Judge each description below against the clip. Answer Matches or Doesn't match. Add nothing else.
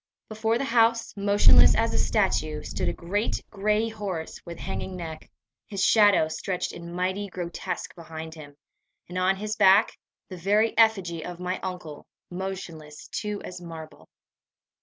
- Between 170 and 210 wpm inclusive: Doesn't match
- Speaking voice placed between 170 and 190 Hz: Matches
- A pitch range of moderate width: Matches